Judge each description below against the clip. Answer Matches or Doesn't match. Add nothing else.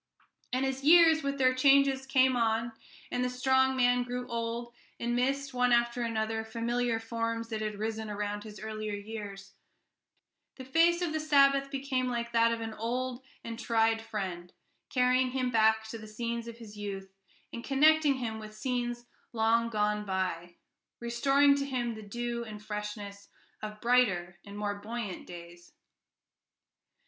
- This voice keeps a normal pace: Matches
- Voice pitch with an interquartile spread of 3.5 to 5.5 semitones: Doesn't match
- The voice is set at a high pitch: Matches